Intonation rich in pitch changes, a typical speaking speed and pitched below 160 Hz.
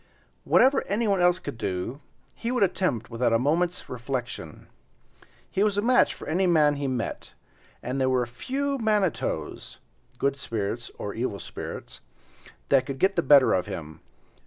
Yes: wide, 8.2 semitones; average, 160 wpm; medium, 140 Hz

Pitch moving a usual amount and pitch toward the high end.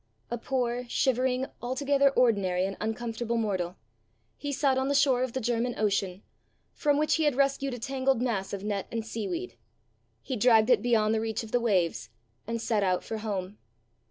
Yes: average, 3.9 semitones; high, 230 Hz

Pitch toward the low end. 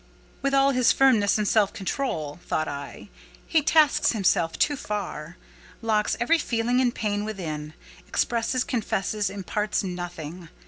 No: high, 210 Hz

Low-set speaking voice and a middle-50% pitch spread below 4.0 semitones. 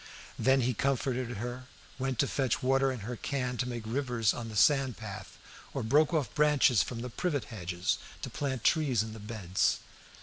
Yes: low, 125 Hz; average, 3.3 semitones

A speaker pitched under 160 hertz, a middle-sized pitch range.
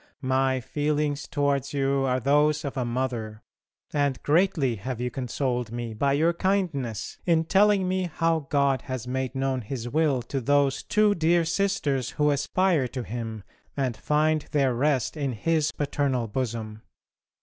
Yes: medium, 140 Hz; average, 3.4 semitones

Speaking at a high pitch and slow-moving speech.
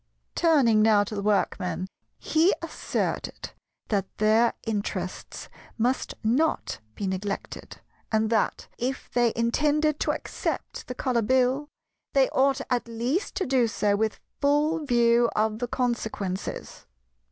Yes: high, 235 Hz; slow, 130 wpm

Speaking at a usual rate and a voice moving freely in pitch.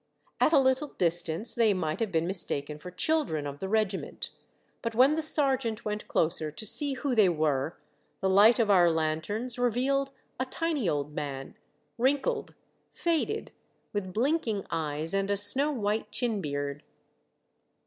Yes: average, 155 wpm; wide, 8.1 semitones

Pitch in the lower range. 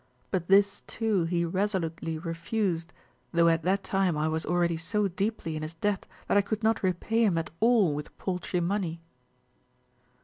No: medium, 180 Hz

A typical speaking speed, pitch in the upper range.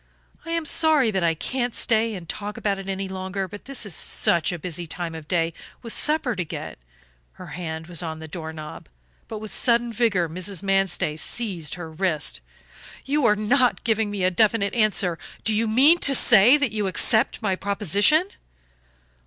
Yes: average, 190 wpm; high, 200 Hz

